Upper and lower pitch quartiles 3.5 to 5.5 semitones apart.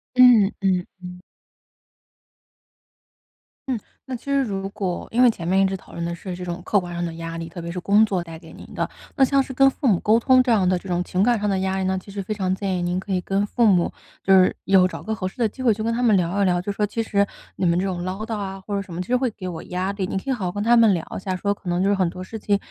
No: average, 3.1 semitones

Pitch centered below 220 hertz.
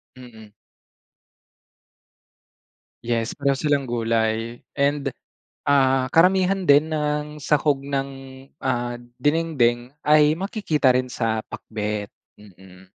Yes: low, 135 Hz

